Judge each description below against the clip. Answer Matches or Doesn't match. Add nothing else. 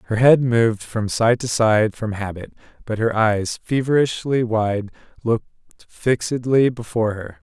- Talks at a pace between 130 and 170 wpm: Matches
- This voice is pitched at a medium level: Doesn't match